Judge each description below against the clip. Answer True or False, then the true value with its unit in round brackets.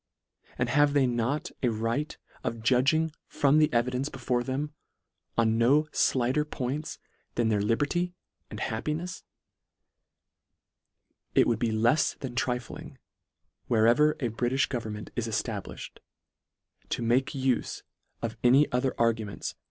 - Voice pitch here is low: True (125 Hz)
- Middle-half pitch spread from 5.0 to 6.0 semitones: False (3.6 semitones)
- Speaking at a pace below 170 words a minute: True (140 wpm)